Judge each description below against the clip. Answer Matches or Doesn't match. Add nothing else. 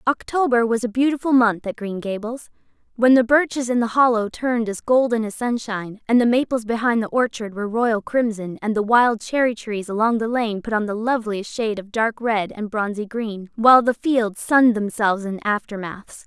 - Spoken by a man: Doesn't match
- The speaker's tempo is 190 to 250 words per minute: Matches